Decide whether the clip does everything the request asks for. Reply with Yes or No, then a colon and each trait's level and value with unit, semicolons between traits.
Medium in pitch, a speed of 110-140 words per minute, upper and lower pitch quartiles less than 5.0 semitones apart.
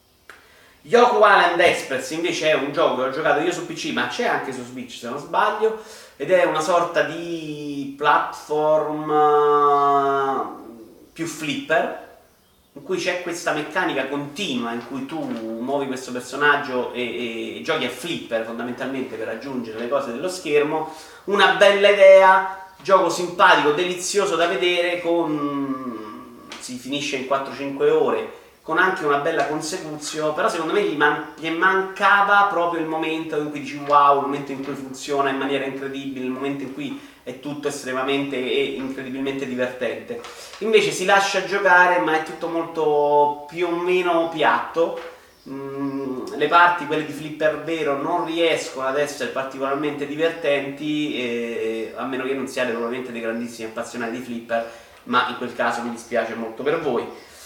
No: medium, 145 Hz; average, 160 wpm; average, 4.5 semitones